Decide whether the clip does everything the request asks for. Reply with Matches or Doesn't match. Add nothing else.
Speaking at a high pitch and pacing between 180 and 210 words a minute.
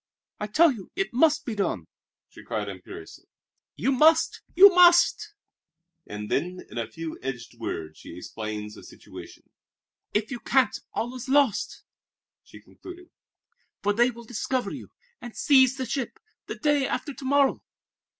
Doesn't match